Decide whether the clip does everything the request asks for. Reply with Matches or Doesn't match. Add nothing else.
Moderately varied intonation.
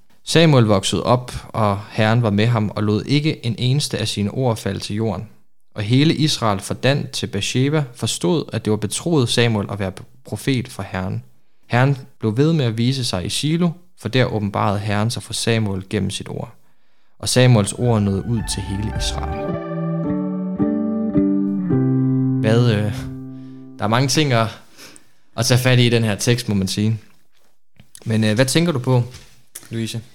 Matches